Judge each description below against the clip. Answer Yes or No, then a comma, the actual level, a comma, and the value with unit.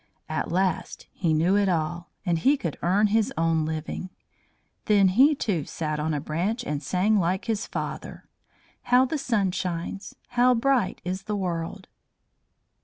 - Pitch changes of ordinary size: Yes, average, 4.6 semitones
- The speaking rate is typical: Yes, average, 160 wpm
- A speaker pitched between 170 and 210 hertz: Yes, medium, 185 Hz